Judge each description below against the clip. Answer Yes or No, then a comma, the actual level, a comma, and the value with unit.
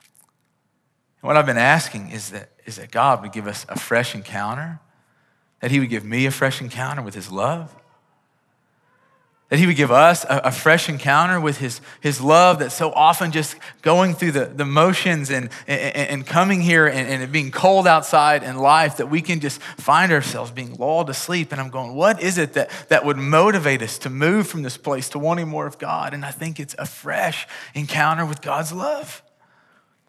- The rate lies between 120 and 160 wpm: No, average, 200 wpm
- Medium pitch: Yes, medium, 150 Hz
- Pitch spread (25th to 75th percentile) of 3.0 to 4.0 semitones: Yes, average, 3.6 semitones